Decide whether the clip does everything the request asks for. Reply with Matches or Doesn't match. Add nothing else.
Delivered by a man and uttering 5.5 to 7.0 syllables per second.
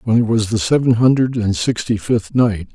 Doesn't match